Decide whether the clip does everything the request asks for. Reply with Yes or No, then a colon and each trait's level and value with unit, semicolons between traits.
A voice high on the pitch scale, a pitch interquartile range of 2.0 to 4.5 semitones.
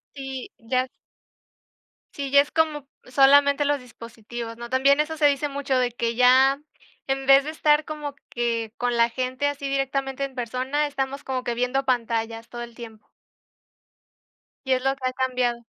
Yes: very high, 265 Hz; average, 2.7 semitones